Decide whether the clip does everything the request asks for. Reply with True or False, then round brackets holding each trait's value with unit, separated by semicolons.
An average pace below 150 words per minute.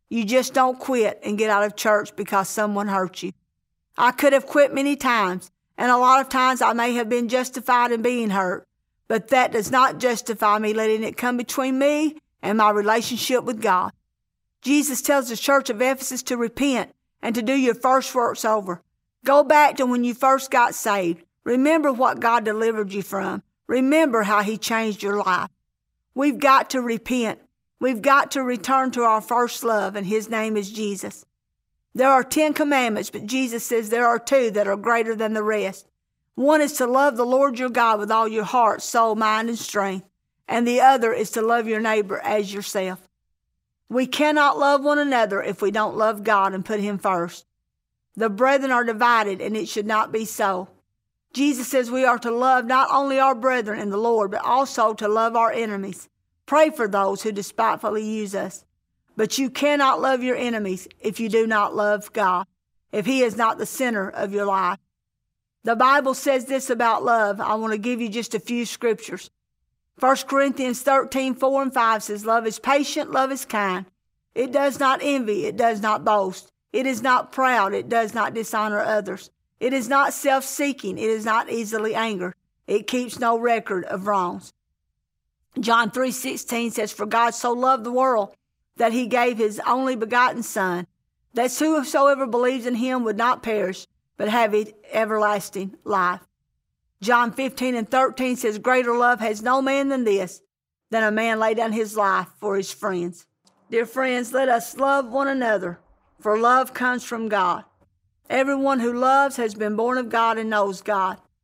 False (185 wpm)